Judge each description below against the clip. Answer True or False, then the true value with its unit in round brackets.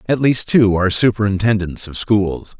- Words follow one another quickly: False (160 wpm)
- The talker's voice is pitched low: True (105 Hz)